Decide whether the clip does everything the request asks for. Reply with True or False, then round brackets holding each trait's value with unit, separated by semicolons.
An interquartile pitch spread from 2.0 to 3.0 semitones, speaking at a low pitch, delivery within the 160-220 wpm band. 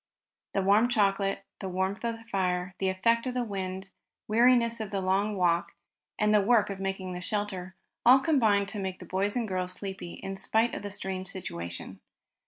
False (2.7 semitones; 195 Hz; 190 wpm)